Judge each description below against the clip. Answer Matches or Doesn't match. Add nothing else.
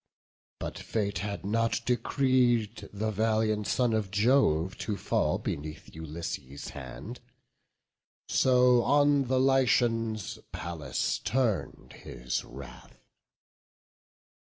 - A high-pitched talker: Doesn't match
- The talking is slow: Matches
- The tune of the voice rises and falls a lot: Doesn't match